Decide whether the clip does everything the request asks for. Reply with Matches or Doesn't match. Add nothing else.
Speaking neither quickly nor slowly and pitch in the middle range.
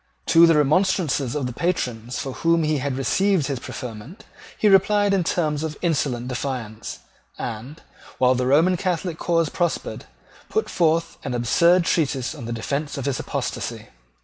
Matches